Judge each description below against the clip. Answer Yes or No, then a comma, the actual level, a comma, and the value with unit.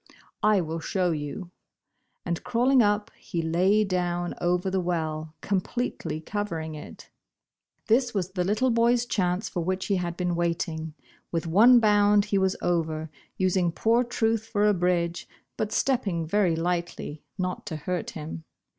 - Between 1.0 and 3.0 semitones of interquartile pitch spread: No, average, 3.7 semitones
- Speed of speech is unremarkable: Yes, average, 155 wpm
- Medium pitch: Yes, medium, 180 Hz